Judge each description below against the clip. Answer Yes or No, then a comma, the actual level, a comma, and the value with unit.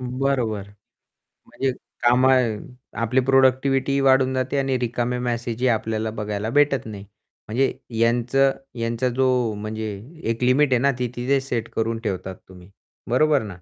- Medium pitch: No, low, 125 Hz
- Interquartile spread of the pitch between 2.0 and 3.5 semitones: Yes, average, 2.8 semitones